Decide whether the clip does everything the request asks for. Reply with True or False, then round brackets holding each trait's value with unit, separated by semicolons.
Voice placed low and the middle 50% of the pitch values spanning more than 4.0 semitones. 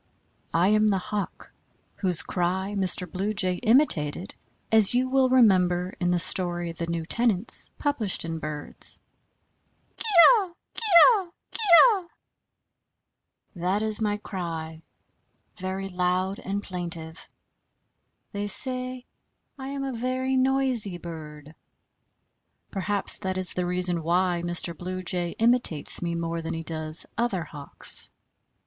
False (185 Hz; 4.5 semitones)